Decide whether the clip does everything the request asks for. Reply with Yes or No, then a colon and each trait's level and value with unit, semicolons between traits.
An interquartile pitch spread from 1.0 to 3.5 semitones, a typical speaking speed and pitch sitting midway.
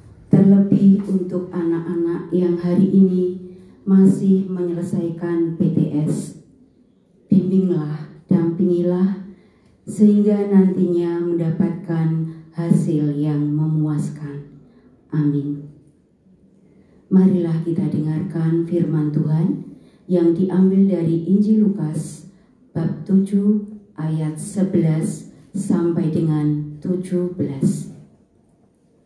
No: average, 2.8 semitones; slow, 70 wpm; medium, 175 Hz